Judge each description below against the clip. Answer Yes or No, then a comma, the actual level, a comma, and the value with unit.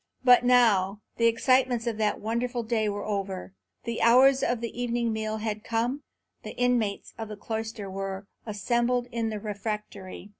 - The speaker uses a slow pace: No, average, 160 wpm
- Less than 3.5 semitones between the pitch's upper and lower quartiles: Yes, narrow, 2.4 semitones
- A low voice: No, high, 225 Hz